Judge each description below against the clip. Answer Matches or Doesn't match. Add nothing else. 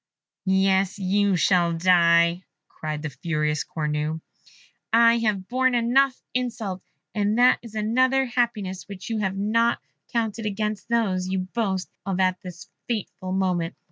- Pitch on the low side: Doesn't match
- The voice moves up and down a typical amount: Matches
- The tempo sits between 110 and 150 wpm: Matches